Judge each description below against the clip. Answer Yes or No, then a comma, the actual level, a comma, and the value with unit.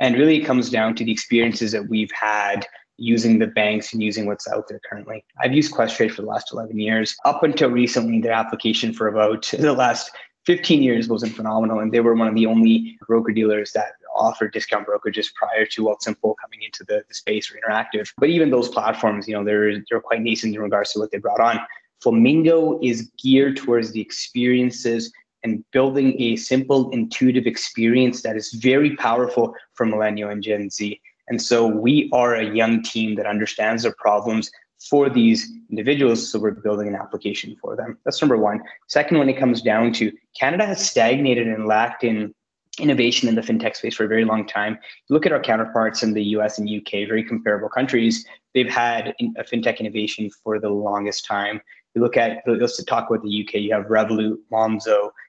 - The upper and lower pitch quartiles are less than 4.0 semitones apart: Yes, narrow, 2.5 semitones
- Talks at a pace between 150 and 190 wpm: No, average, 200 wpm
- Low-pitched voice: Yes, low, 115 Hz